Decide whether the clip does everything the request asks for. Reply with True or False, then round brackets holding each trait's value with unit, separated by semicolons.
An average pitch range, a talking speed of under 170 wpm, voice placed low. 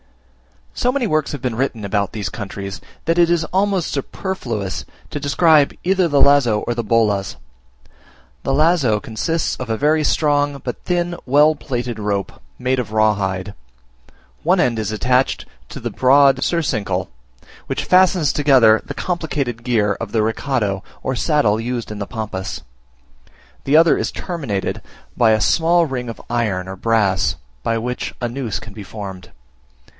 False (5.8 semitones; 160 wpm; 120 Hz)